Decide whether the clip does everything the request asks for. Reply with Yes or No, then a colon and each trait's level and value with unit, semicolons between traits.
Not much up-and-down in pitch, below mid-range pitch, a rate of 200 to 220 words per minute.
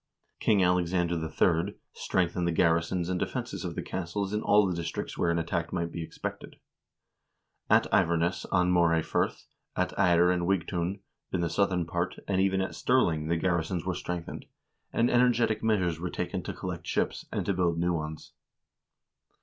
No: narrow, 2.0 semitones; very low, 90 Hz; average, 175 wpm